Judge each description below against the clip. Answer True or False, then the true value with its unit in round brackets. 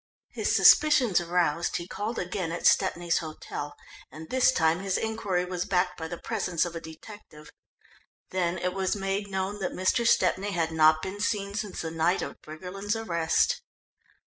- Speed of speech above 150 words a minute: True (170 wpm)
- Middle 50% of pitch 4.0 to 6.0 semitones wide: False (3.3 semitones)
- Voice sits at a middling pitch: True (180 Hz)